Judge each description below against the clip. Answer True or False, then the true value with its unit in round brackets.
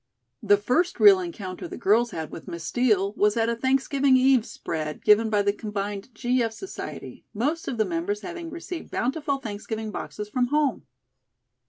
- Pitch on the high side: True (230 Hz)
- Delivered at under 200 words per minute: True (175 wpm)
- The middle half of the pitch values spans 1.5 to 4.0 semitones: False (4.9 semitones)